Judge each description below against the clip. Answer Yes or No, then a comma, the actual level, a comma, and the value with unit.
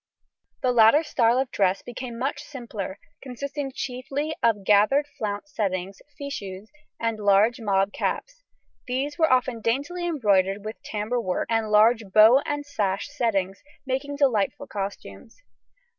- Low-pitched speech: No, high, 230 Hz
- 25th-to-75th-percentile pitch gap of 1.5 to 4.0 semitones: No, average, 5.3 semitones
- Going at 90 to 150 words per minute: Yes, slow, 135 wpm